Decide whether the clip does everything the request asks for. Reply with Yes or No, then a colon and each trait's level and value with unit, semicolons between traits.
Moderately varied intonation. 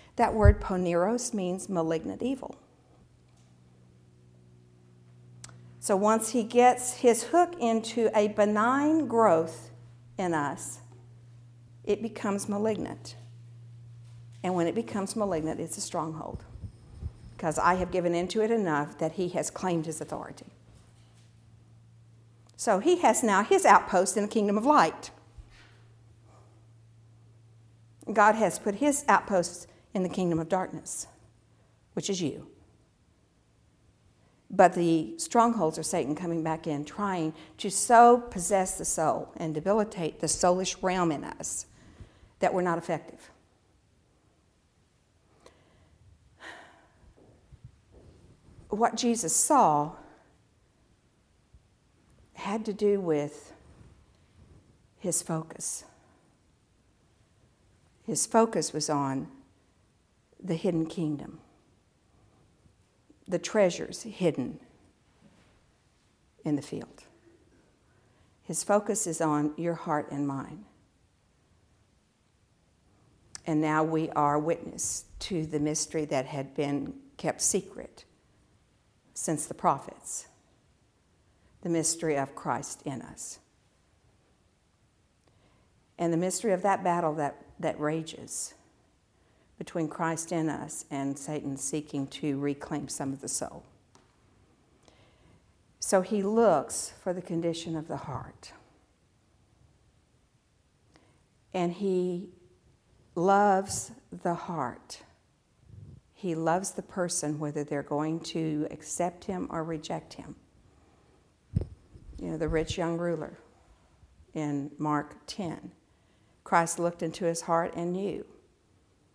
No: wide, 7.8 semitones